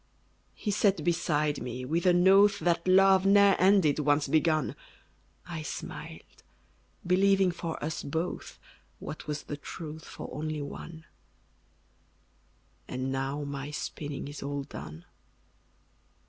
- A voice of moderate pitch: Yes, medium, 160 Hz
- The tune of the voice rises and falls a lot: No, average, 4.0 semitones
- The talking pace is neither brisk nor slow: No, slow, 120 wpm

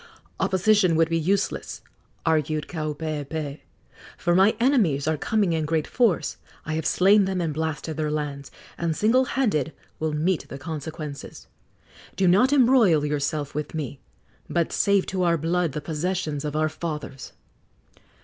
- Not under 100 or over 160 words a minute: Yes, average, 150 wpm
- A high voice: No, medium, 160 Hz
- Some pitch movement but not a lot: Yes, average, 3.7 semitones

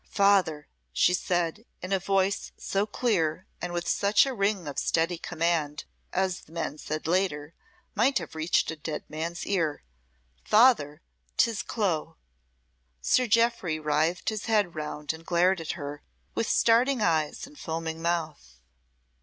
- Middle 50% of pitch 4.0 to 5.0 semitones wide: Yes, average, 4.3 semitones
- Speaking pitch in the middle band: Yes, medium, 175 Hz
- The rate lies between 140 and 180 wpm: Yes, average, 145 wpm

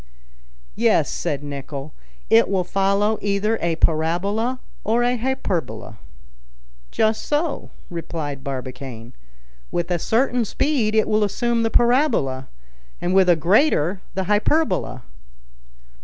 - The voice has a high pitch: Yes, high, 195 Hz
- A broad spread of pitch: Yes, wide, 6.8 semitones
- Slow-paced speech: Yes, slow, 115 wpm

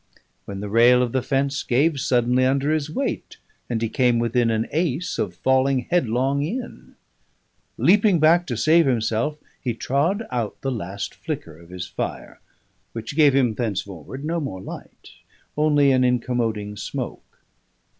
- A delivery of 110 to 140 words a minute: No, average, 155 wpm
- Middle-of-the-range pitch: No, low, 130 Hz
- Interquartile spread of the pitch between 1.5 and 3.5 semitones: No, average, 4.4 semitones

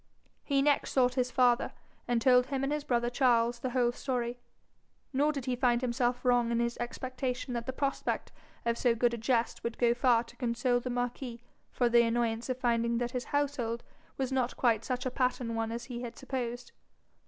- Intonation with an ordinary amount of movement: No, narrow, 1.5 semitones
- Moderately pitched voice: No, high, 245 Hz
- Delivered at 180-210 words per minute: Yes, average, 200 wpm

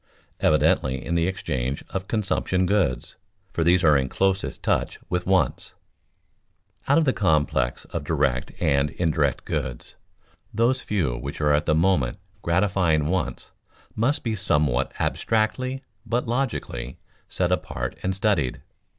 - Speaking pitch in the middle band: No, very low, 85 Hz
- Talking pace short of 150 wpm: Yes, slow, 135 wpm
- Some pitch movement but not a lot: No, wide, 6.6 semitones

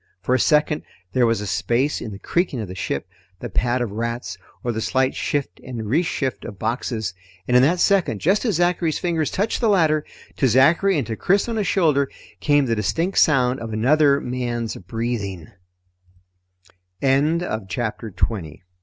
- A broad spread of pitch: Yes, wide, 5.9 semitones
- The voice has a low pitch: Yes, low, 130 Hz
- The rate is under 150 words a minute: No, average, 165 wpm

